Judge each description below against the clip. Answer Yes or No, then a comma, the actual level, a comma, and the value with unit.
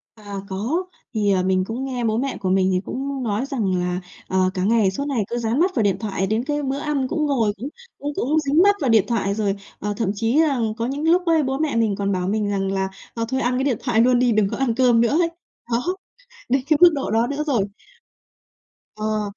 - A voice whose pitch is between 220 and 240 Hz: Yes, high, 235 Hz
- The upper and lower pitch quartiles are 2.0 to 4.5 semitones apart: No, average, 5.2 semitones